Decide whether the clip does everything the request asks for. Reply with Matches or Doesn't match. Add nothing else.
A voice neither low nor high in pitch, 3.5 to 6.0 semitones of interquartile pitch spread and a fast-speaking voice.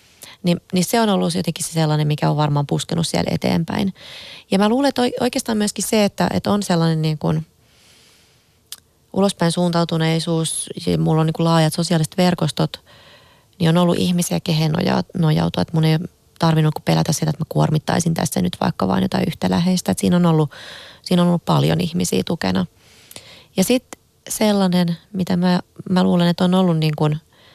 Doesn't match